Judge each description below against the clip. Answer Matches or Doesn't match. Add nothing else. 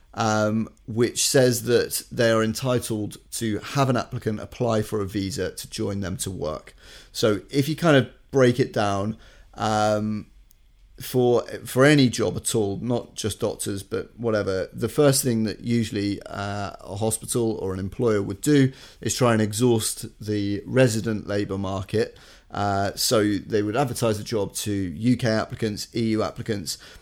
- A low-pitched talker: Matches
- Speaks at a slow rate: Doesn't match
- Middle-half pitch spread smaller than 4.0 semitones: Matches